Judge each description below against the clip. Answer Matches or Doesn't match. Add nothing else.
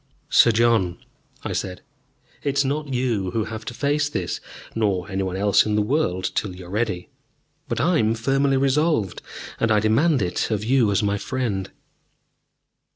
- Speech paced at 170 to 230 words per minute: Matches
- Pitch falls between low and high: Doesn't match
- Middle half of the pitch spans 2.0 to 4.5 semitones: Doesn't match